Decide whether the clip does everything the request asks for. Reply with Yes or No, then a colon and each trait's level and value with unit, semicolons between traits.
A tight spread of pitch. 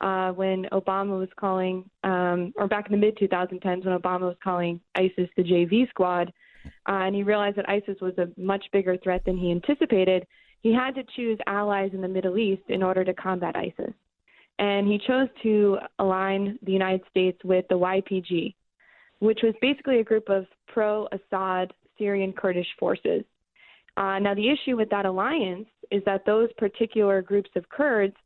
Yes: narrow, 2.1 semitones